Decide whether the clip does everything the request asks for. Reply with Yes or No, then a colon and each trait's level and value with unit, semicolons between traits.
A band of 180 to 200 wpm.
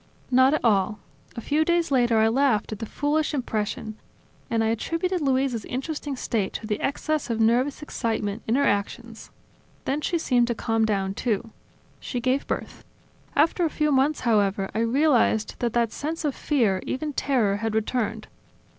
No: average, 170 wpm